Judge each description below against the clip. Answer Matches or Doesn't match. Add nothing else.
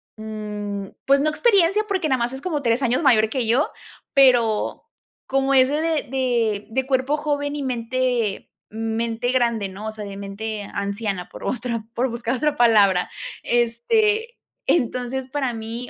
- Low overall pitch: Doesn't match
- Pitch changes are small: Doesn't match